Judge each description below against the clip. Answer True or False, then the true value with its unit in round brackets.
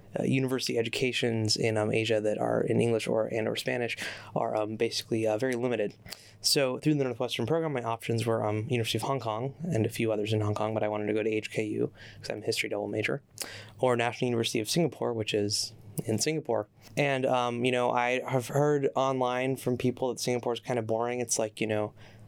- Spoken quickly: True (220 wpm)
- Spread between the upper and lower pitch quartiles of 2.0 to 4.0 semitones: True (2.7 semitones)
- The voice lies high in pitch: False (115 Hz)